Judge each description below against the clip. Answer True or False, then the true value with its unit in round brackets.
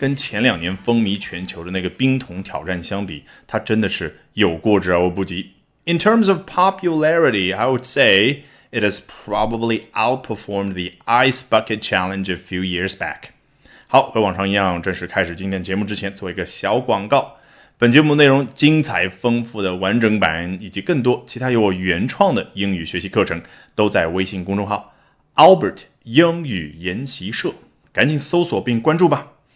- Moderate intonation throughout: False (5.9 semitones)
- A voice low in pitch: True (105 Hz)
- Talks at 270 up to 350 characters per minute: False (390 characters per minute)